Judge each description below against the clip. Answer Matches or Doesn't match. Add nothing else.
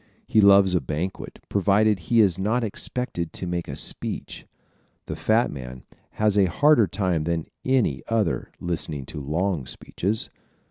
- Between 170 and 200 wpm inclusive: Doesn't match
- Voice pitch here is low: Matches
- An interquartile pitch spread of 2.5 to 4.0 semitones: Doesn't match